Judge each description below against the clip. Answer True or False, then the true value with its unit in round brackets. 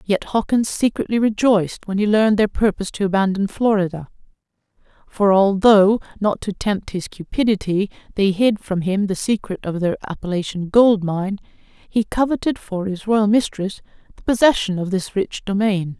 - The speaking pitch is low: False (200 Hz)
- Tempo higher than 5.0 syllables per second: False (4.9 syllables/s)